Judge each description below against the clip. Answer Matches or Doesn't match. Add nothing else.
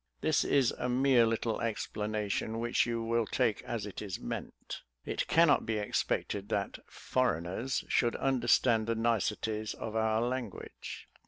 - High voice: Doesn't match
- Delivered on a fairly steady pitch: Matches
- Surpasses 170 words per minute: Doesn't match